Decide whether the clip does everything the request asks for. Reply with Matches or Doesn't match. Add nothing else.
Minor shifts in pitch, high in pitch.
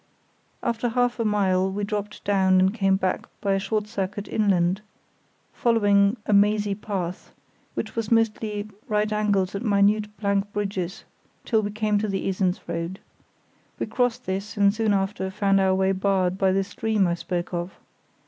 Matches